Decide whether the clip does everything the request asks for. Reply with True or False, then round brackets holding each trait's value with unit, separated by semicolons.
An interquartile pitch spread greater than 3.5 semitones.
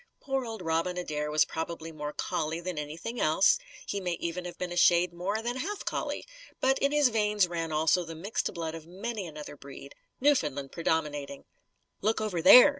True (5.0 semitones)